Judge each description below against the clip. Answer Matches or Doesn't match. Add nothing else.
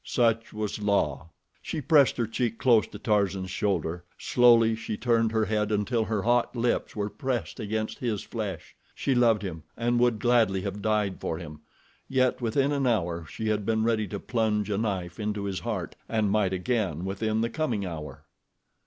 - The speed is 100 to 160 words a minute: Doesn't match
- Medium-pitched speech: Doesn't match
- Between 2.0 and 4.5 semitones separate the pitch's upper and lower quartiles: Matches